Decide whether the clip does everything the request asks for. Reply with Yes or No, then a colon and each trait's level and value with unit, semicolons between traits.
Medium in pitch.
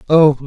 Yes: medium, 145 Hz